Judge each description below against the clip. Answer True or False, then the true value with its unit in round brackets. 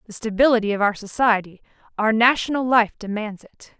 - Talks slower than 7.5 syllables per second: True (5.5 syllables/s)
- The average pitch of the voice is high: True (220 Hz)